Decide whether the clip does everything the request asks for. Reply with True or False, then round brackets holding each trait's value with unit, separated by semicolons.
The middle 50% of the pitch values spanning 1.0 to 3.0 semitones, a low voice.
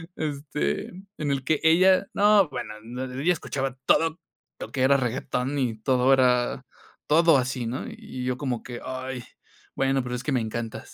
True (2.7 semitones; 130 Hz)